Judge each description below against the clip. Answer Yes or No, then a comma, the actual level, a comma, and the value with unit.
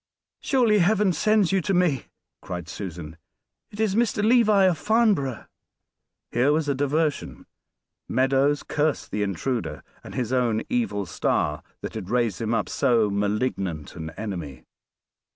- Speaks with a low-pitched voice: Yes, low, 130 Hz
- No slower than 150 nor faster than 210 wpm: No, average, 140 wpm